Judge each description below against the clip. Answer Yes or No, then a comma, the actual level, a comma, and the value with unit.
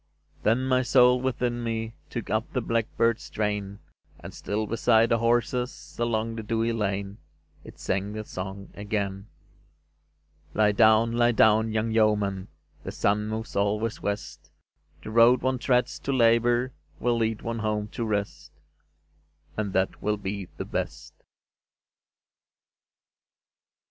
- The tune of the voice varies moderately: No, narrow, 2.2 semitones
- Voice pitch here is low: Yes, low, 110 Hz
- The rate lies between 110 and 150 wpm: Yes, slow, 135 wpm